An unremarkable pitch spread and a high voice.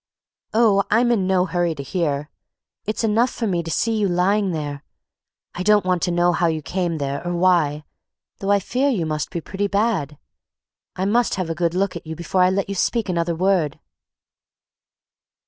No: average, 3.4 semitones; medium, 180 Hz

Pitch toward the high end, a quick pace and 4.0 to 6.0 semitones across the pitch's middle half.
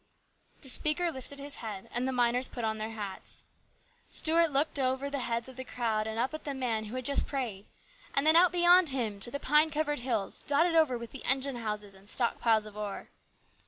Yes: very high, 255 Hz; fast, 230 wpm; average, 4.5 semitones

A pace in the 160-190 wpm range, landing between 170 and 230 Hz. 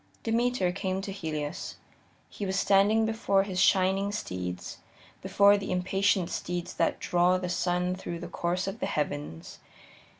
No: average, 145 wpm; medium, 185 Hz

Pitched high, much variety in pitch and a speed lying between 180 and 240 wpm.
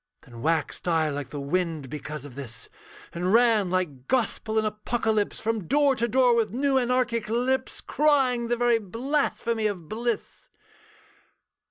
No: high, 220 Hz; wide, 6.6 semitones; average, 150 wpm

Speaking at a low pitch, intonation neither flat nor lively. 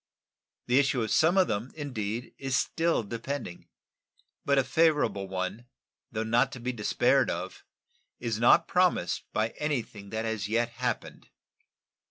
Yes: low, 120 Hz; average, 4.1 semitones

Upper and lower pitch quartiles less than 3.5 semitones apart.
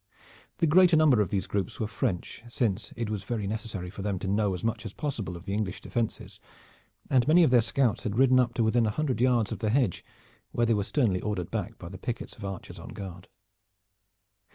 No: average, 3.8 semitones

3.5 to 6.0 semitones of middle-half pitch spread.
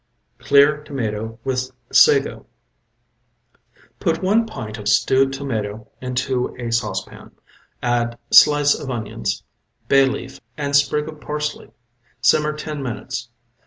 Yes: average, 4.1 semitones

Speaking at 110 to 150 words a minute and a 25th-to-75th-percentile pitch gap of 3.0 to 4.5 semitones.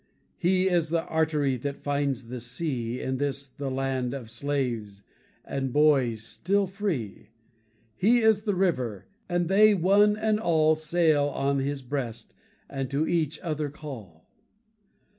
No: average, 140 wpm; average, 5.1 semitones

